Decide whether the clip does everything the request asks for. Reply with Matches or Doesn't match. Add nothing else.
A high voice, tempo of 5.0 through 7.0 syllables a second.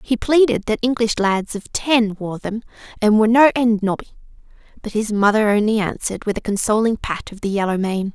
Matches